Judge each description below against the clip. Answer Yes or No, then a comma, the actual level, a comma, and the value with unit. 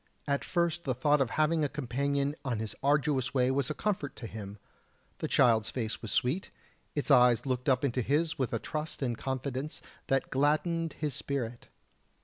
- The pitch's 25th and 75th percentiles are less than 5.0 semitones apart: Yes, average, 3.1 semitones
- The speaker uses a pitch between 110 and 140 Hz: Yes, low, 135 Hz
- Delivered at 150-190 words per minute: Yes, average, 180 wpm